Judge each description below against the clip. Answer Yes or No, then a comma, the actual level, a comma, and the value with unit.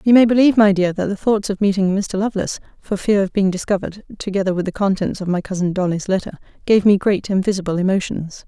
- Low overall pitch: No, high, 195 Hz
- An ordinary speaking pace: No, fast, 225 wpm